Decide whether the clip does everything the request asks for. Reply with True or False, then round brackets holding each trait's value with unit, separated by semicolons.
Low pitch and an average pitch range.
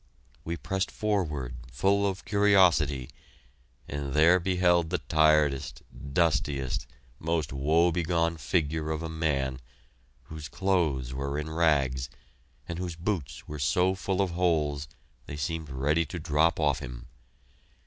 True (80 Hz; 3.8 semitones)